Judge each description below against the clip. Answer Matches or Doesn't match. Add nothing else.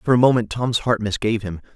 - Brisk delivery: Matches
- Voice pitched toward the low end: Matches